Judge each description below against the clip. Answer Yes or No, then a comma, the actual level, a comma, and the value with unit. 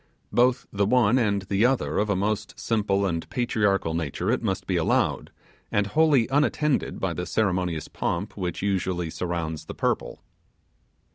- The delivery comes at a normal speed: Yes, average, 155 wpm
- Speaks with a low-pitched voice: Yes, low, 100 Hz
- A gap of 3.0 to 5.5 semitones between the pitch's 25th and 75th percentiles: Yes, average, 4.4 semitones